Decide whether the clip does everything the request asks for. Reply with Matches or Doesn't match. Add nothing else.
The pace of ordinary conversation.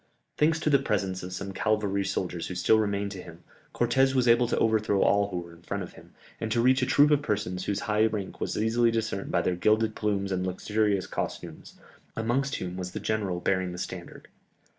Doesn't match